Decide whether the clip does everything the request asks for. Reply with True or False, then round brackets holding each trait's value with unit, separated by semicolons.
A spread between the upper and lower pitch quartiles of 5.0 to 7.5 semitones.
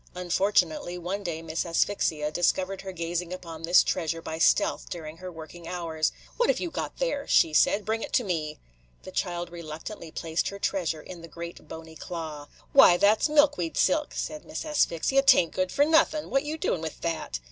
False (4.1 semitones)